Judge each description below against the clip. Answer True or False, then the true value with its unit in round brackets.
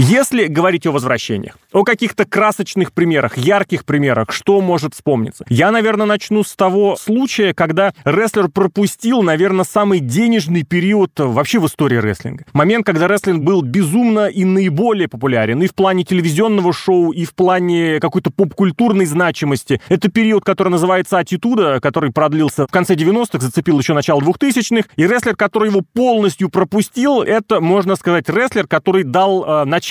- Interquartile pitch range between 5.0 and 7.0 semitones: False (4.2 semitones)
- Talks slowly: False (155 wpm)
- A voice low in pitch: False (185 Hz)